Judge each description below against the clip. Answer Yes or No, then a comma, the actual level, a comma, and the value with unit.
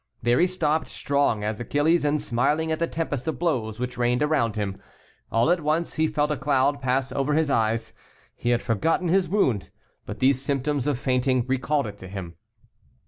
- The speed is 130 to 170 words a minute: No, average, 195 wpm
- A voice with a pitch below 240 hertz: Yes, medium, 140 Hz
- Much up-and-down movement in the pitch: No, average, 4.2 semitones